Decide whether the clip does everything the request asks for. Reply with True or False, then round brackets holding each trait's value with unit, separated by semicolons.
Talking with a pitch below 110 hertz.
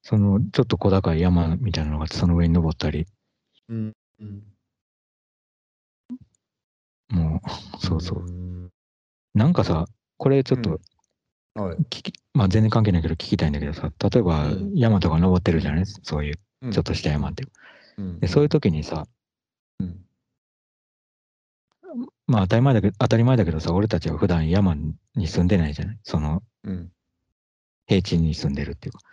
True (90 Hz)